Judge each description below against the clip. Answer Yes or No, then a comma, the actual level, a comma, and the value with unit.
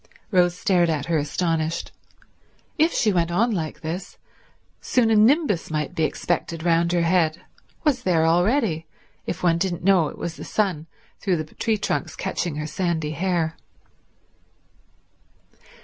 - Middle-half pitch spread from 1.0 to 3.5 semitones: Yes, average, 3.1 semitones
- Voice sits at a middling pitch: Yes, medium, 175 Hz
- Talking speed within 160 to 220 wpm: No, average, 150 wpm